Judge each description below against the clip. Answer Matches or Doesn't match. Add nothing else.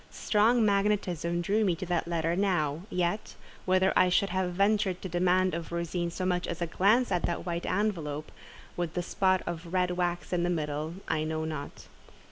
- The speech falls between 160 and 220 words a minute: Matches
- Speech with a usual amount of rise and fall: Doesn't match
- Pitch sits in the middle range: Matches